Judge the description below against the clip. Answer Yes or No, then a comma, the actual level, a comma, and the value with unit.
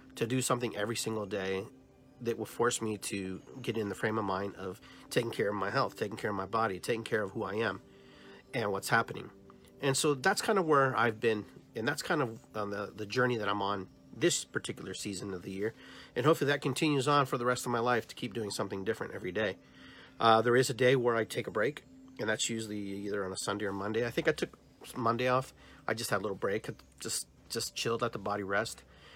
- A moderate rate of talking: No, fast, 245 wpm